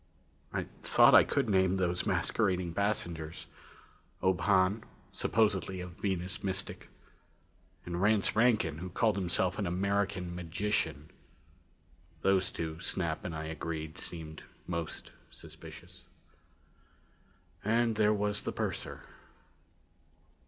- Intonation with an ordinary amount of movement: Yes, average, 3.2 semitones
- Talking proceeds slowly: Yes, slow, 110 wpm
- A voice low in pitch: Yes, very low, 95 Hz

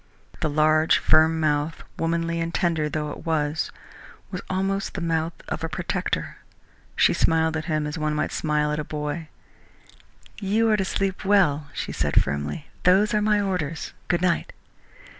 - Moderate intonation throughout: Yes, average, 3.3 semitones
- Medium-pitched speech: Yes, medium, 160 Hz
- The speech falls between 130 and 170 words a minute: Yes, average, 165 wpm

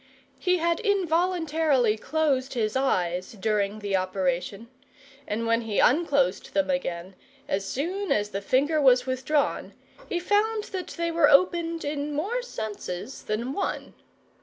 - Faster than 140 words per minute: No, slow, 135 wpm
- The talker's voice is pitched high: Yes, very high, 275 Hz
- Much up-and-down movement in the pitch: Yes, wide, 7.9 semitones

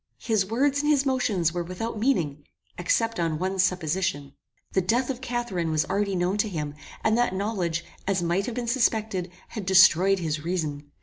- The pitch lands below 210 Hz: Yes, high, 190 Hz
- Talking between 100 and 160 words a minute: No, average, 180 wpm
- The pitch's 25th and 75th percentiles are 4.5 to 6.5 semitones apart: Yes, average, 5.1 semitones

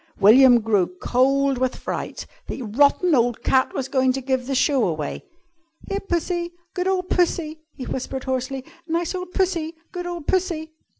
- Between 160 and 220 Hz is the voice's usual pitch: No, very high, 275 Hz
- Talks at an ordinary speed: Yes, average, 165 wpm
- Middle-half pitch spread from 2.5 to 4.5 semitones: No, average, 5.3 semitones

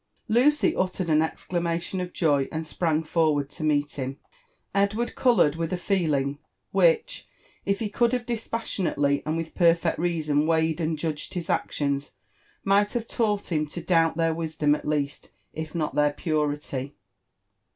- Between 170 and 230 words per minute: No, average, 155 wpm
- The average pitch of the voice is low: No, medium, 165 Hz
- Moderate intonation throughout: Yes, average, 4.0 semitones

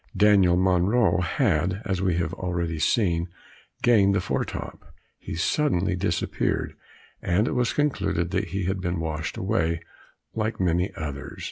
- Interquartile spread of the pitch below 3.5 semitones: Yes, average, 2.7 semitones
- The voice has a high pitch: No, very low, 90 Hz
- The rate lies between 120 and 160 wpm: Yes, average, 145 wpm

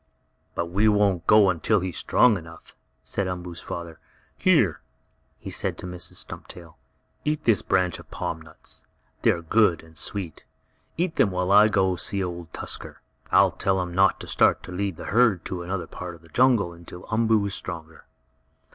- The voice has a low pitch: Yes, very low, 90 Hz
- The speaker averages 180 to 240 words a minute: Yes, average, 185 wpm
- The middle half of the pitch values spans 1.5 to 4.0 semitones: Yes, average, 3.0 semitones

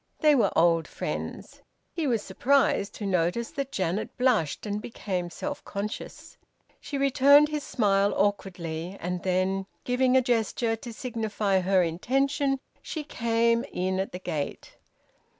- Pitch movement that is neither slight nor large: No, wide, 5.7 semitones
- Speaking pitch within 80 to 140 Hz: No, high, 215 Hz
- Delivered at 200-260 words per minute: No, average, 140 wpm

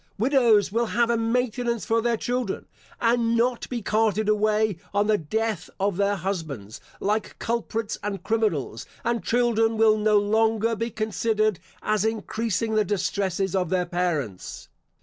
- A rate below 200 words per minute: Yes, average, 150 wpm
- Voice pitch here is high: Yes, high, 215 Hz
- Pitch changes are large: No, narrow, 2.5 semitones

